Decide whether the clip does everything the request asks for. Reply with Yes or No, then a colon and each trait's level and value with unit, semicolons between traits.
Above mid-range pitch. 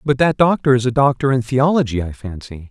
No: low, 125 Hz